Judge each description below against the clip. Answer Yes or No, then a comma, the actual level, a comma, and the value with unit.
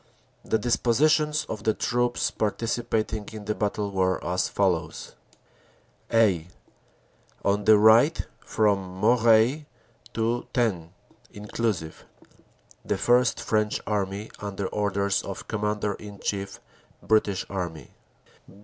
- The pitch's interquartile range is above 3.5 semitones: No, narrow, 2.4 semitones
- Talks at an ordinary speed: No, slow, 110 wpm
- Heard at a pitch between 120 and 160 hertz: No, low, 105 Hz